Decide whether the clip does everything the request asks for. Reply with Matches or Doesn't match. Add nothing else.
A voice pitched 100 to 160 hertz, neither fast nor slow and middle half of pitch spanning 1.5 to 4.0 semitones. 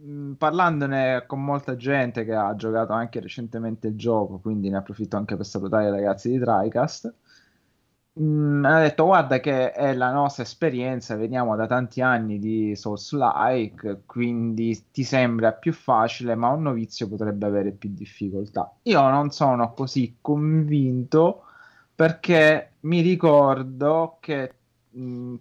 Doesn't match